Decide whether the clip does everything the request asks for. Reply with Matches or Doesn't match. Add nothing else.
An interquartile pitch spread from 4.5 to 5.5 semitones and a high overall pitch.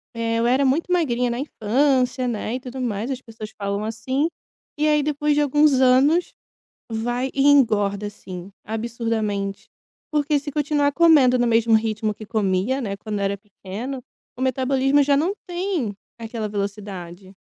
Matches